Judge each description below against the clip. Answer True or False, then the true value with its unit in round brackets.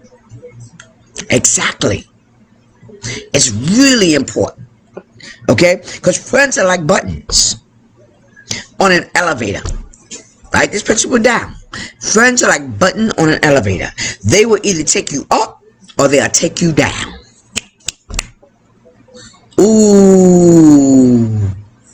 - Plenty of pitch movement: True (8.2 semitones)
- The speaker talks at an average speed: False (100 wpm)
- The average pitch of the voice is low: False (145 Hz)